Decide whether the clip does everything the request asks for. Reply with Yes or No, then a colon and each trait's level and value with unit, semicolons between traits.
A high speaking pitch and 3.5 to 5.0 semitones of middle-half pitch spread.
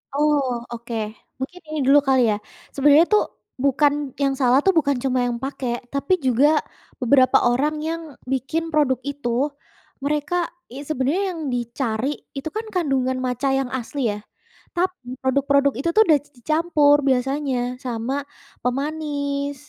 No: very high, 280 Hz; average, 2.7 semitones